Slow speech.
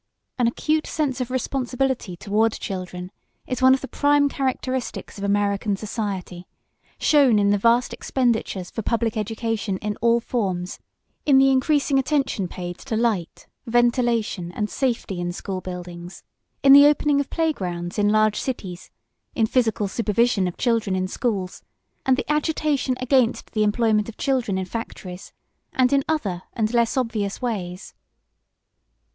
No: average, 150 wpm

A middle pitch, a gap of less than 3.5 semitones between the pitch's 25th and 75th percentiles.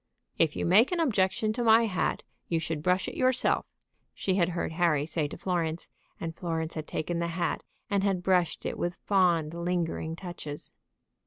Yes: medium, 175 Hz; average, 2.9 semitones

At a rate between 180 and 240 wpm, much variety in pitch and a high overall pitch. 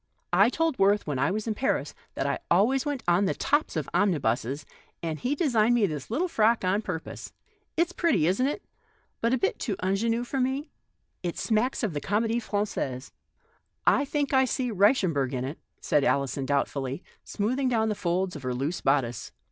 Yes: average, 190 wpm; wide, 8.5 semitones; high, 205 Hz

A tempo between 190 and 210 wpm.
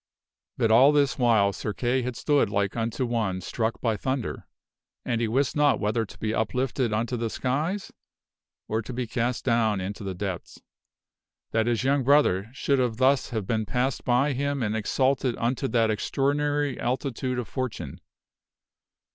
No: average, 165 wpm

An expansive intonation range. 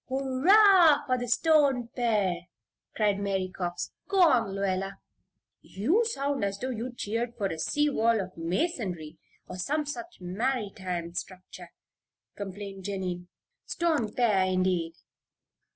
Yes: wide, 6.4 semitones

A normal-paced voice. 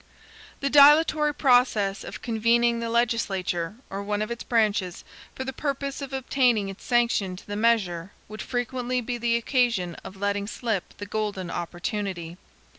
Yes: average, 155 wpm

